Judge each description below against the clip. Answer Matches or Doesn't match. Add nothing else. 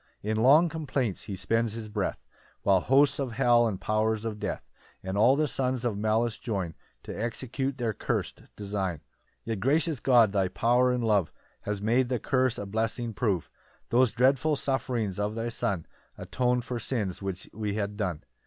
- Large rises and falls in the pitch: Doesn't match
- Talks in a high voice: Doesn't match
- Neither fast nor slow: Matches